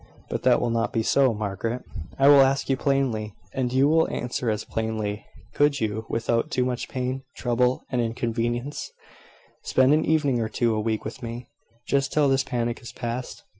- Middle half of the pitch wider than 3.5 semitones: No, average, 2.8 semitones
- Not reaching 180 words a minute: No, average, 185 wpm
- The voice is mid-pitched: No, low, 120 Hz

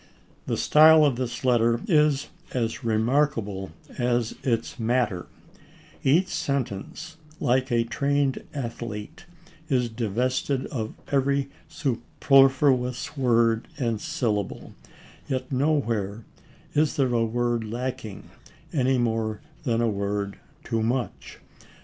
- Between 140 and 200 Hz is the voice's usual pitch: No, low, 120 Hz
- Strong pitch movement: No, average, 3.1 semitones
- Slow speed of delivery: Yes, slow, 105 wpm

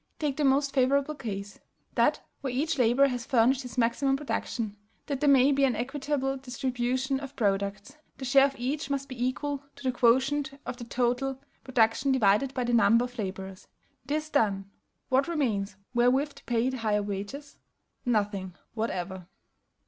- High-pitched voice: Yes, very high, 255 Hz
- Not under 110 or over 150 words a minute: No, average, 165 wpm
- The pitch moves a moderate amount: Yes, average, 3.4 semitones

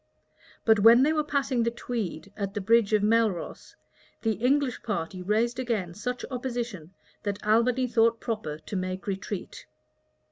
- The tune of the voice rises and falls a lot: No, average, 3.5 semitones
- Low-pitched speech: No, high, 225 Hz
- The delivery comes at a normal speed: Yes, average, 155 wpm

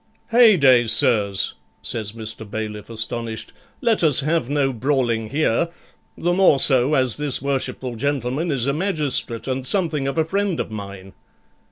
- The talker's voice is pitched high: No, low, 135 Hz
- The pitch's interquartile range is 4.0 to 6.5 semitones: Yes, average, 5.2 semitones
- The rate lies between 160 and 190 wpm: No, average, 150 wpm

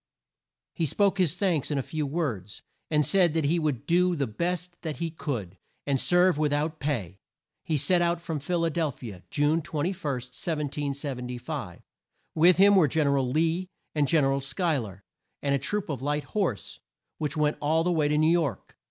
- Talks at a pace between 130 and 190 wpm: No, average, 200 wpm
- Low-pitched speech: No, medium, 150 Hz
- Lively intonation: No, average, 3.6 semitones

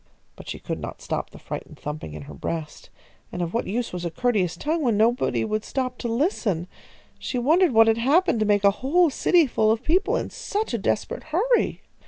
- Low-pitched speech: No, high, 235 Hz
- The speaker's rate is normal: No, fast, 215 wpm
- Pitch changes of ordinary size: No, wide, 7.6 semitones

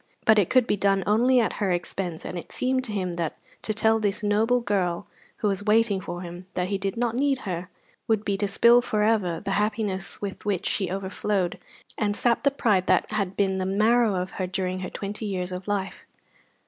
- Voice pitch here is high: Yes, high, 200 Hz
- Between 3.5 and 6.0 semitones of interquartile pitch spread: No, average, 2.9 semitones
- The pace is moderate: No, fast, 215 wpm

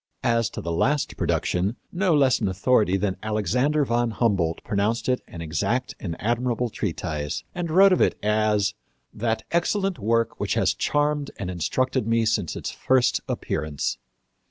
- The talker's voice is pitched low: Yes, low, 115 Hz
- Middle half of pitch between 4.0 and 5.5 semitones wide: Yes, average, 4.6 semitones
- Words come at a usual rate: Yes, average, 155 wpm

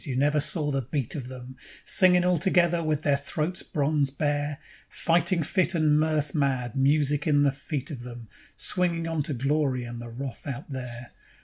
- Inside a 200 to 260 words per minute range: No, average, 185 wpm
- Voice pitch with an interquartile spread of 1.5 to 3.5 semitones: Yes, average, 3.0 semitones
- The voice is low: No, medium, 145 Hz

